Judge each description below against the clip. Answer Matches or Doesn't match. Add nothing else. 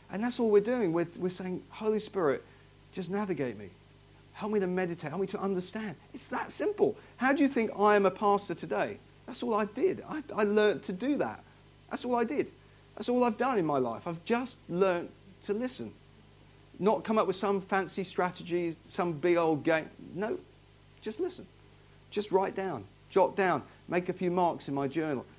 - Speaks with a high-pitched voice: Matches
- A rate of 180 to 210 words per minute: Matches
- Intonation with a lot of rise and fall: Doesn't match